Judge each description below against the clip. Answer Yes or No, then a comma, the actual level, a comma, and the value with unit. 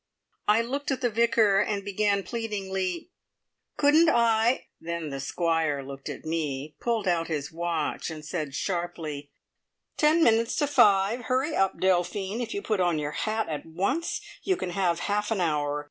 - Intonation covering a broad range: Yes, wide, 5.9 semitones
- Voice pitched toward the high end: Yes, high, 195 Hz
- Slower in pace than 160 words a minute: No, average, 170 wpm